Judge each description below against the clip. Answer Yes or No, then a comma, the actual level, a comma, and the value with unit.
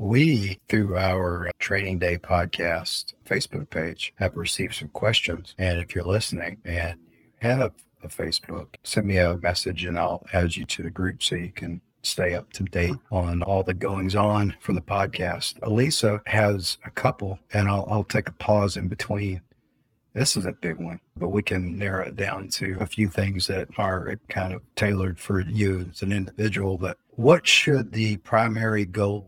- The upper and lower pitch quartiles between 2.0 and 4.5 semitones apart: Yes, average, 2.7 semitones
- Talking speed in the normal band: Yes, average, 185 wpm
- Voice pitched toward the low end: Yes, very low, 95 Hz